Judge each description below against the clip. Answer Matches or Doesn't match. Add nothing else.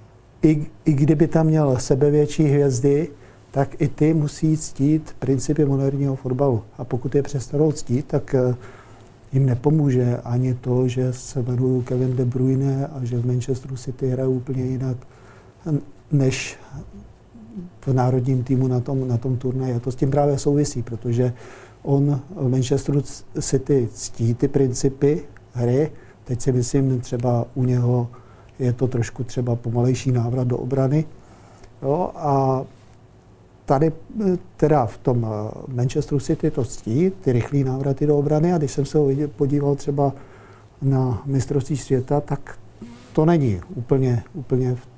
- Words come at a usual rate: Matches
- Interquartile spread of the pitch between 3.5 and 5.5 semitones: Doesn't match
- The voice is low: Matches